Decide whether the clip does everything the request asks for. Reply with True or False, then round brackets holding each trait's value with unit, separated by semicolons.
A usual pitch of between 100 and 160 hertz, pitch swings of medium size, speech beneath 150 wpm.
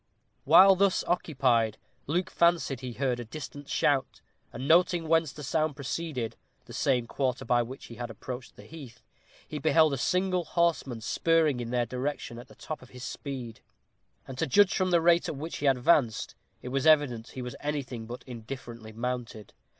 False (135 Hz; 4.7 semitones; 180 wpm)